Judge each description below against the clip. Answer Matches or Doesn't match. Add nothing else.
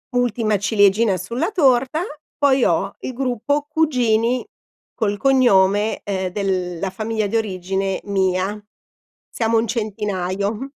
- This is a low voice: Doesn't match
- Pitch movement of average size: Matches